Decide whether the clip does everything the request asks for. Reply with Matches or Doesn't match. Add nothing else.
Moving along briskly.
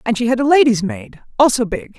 Matches